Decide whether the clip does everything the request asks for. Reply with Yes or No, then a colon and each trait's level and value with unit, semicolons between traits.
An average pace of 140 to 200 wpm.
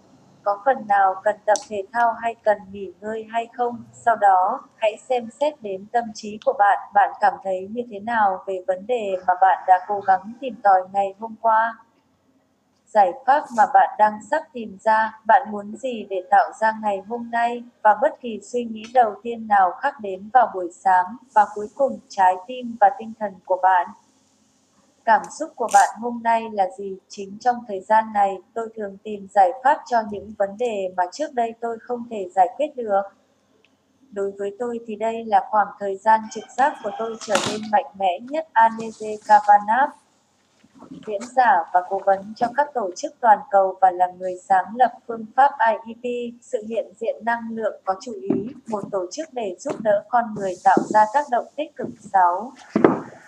Yes: average, 195 wpm